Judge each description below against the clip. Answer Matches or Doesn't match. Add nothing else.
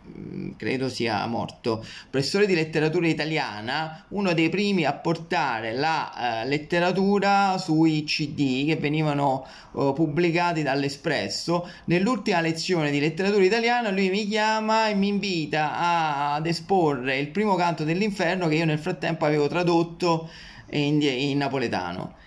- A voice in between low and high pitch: Matches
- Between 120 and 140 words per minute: Matches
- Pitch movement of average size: Matches